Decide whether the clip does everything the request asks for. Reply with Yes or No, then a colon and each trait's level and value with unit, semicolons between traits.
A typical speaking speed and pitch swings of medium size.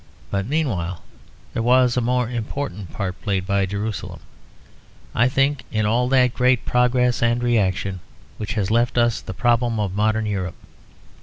Yes: average, 155 wpm; average, 3.7 semitones